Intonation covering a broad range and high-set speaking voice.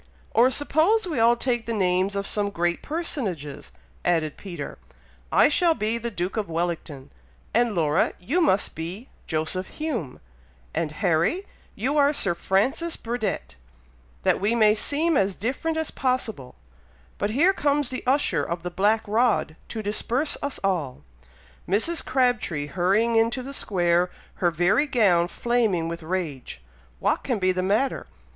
Yes: wide, 6.7 semitones; high, 210 Hz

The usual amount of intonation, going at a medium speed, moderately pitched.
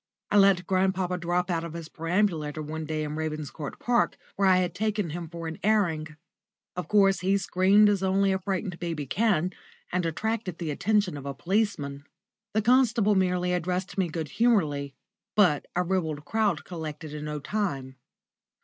Yes: average, 4.1 semitones; average, 170 wpm; medium, 180 Hz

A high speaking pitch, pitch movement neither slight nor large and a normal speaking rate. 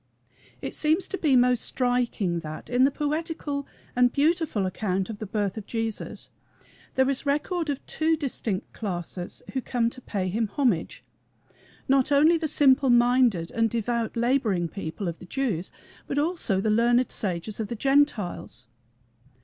No: high, 240 Hz; wide, 5.8 semitones; average, 155 wpm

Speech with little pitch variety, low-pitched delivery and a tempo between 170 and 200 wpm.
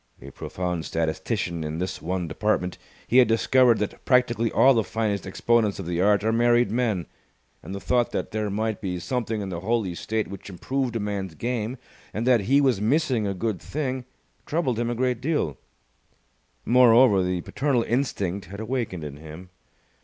No: average, 4.6 semitones; low, 110 Hz; average, 180 wpm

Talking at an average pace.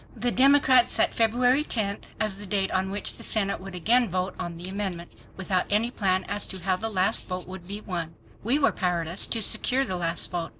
No: fast, 215 wpm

